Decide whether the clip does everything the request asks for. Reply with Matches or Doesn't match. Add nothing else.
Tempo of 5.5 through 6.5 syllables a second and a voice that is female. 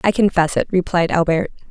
Matches